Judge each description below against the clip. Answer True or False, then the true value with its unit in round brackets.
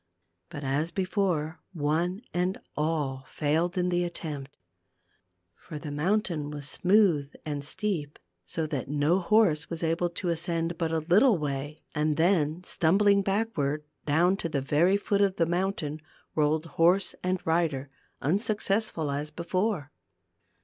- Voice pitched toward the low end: False (165 Hz)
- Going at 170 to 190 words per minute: False (140 wpm)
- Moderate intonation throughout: True (3.8 semitones)